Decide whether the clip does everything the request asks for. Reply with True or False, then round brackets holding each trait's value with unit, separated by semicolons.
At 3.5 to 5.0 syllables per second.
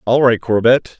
True (4.6 syllables/s)